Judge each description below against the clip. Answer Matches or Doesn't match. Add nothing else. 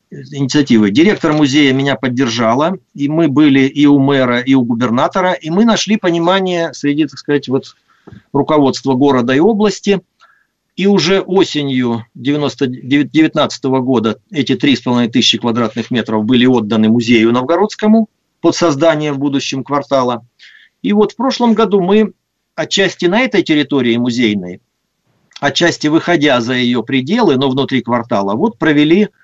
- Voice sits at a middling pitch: Matches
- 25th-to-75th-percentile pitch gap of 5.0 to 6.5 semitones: Matches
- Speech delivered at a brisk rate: Doesn't match